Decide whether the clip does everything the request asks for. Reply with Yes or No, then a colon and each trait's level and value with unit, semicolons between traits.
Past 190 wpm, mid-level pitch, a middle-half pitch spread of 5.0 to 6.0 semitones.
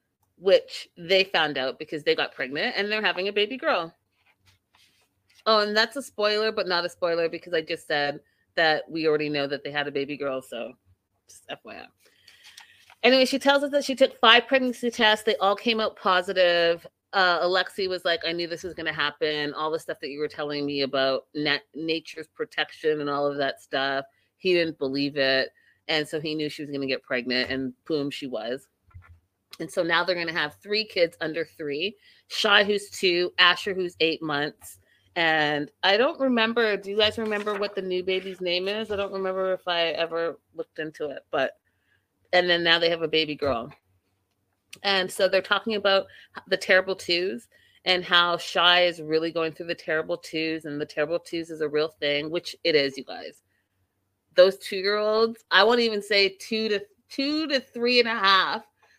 Yes: average, 200 wpm; medium, 170 Hz; average, 5.3 semitones